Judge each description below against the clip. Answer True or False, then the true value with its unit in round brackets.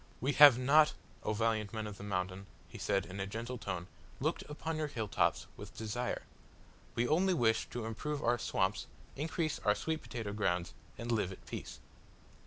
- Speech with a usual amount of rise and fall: False (5.9 semitones)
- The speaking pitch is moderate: False (115 Hz)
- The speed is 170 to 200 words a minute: True (185 wpm)